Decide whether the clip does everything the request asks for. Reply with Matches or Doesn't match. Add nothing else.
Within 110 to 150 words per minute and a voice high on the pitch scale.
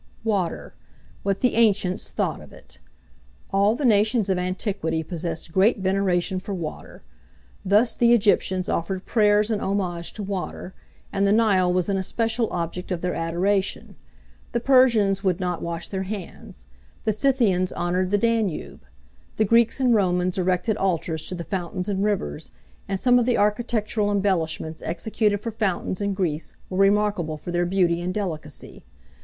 Doesn't match